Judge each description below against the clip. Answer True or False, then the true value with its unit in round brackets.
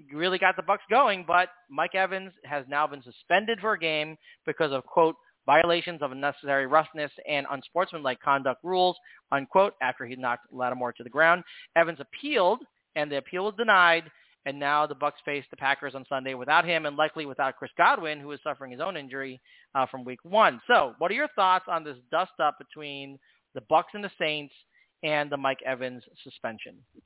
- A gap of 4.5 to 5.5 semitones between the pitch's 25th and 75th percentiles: False (4.1 semitones)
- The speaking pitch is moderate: True (150 Hz)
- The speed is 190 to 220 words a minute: True (195 wpm)